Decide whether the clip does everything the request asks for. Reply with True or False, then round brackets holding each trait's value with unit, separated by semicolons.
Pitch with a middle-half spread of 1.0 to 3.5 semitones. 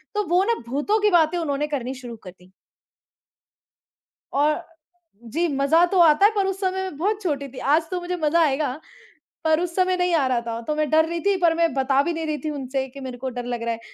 False (4.8 semitones)